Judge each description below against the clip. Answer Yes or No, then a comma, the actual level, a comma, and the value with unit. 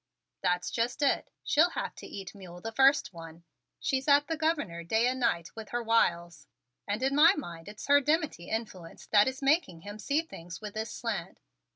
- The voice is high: Yes, high, 225 Hz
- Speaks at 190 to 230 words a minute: Yes, average, 195 wpm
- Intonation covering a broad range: Yes, wide, 8.1 semitones